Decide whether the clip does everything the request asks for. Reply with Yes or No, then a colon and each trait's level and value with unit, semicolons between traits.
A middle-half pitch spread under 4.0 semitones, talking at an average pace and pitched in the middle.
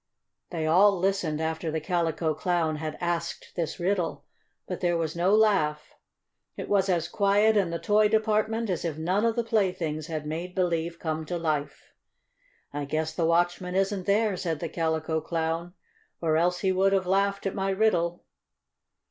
Yes: average, 3.4 semitones; average, 175 wpm; medium, 175 Hz